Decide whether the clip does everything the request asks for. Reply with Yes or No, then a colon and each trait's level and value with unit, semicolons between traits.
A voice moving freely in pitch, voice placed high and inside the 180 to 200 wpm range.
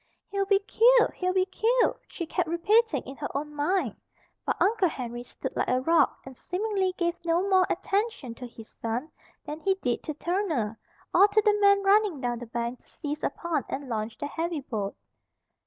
Yes: wide, 7.5 semitones; very high, 335 Hz; average, 190 wpm